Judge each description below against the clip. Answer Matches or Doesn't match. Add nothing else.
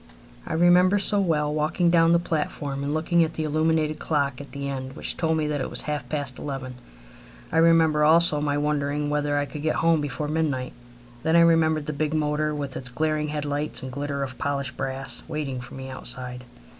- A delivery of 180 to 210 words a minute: Matches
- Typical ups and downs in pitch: Doesn't match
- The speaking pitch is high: Doesn't match